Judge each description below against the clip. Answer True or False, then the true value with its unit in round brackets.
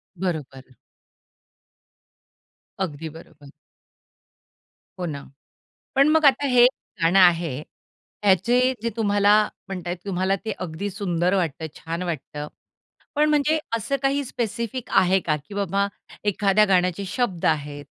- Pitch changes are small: False (5.3 semitones)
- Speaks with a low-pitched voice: False (190 Hz)